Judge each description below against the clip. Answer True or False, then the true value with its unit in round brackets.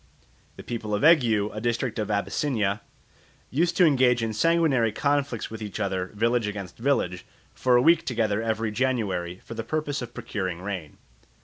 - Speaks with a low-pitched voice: True (115 Hz)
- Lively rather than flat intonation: False (4.2 semitones)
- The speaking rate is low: False (170 wpm)